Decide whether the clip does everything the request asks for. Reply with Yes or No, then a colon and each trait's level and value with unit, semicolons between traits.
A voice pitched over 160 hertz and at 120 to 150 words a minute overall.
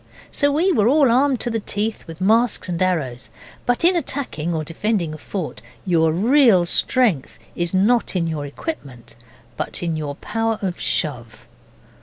No: medium, 185 Hz; average, 165 wpm